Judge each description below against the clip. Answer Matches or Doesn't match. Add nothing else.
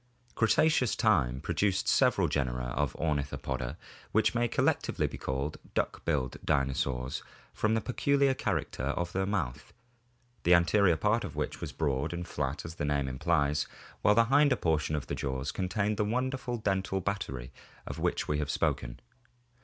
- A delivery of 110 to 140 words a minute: Doesn't match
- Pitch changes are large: Matches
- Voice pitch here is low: Matches